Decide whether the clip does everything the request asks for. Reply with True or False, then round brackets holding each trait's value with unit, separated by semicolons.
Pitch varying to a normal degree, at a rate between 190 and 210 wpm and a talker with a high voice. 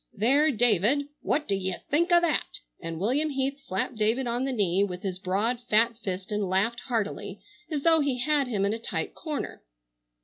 False (5.8 semitones; 195 wpm; 235 Hz)